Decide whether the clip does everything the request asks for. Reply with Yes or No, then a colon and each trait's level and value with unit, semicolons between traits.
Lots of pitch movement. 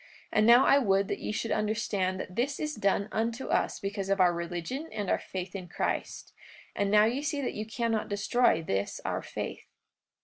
No: average, 3.7 semitones